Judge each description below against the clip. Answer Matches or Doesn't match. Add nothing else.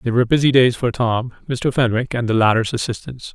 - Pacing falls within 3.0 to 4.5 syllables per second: Doesn't match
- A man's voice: Matches